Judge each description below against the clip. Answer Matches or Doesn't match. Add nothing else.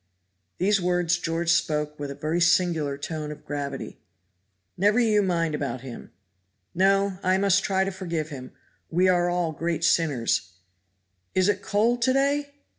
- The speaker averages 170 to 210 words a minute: Doesn't match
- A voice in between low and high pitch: Matches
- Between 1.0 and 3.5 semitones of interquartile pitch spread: Doesn't match